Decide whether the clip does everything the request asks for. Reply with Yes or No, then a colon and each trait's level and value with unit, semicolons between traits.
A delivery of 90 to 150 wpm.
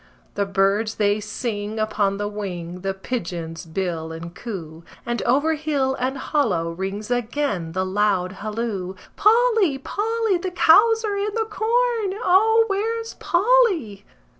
Yes: average, 140 wpm